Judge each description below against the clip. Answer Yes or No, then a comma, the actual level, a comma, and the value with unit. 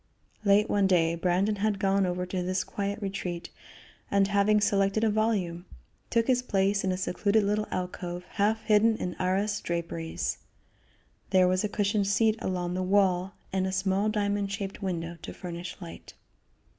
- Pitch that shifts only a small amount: Yes, narrow, 2.2 semitones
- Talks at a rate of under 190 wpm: Yes, average, 165 wpm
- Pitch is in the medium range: No, high, 195 Hz